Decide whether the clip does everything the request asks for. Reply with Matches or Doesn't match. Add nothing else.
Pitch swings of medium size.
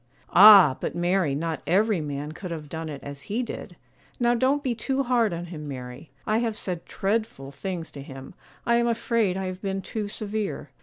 Doesn't match